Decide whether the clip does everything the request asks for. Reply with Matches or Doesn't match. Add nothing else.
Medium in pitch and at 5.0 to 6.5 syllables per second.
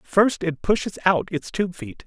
Doesn't match